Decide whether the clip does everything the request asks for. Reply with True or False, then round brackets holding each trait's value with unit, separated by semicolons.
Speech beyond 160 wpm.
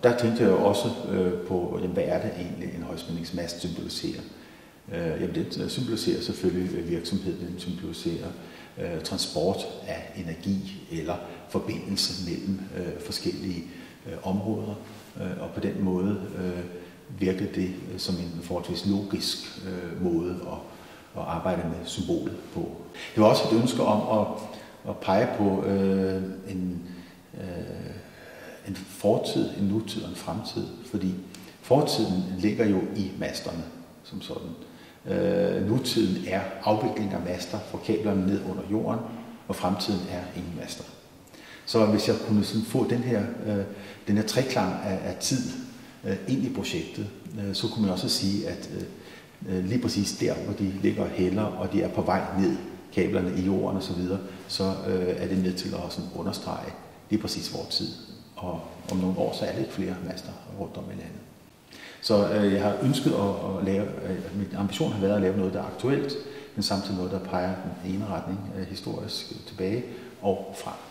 True (170 wpm)